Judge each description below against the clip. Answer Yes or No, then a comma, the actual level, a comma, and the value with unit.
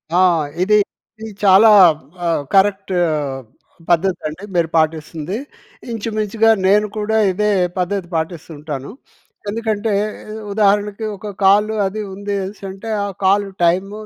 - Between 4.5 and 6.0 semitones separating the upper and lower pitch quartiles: No, average, 3.4 semitones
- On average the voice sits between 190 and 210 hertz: Yes, high, 195 Hz